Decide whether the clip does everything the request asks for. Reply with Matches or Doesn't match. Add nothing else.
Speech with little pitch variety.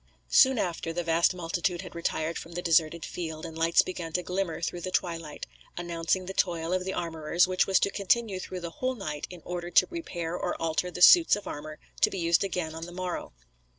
Matches